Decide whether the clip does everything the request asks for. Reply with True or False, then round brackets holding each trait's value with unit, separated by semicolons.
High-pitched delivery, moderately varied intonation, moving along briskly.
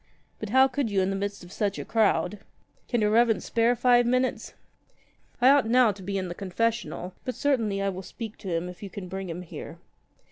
True (210 Hz; 4.0 semitones; 225 wpm)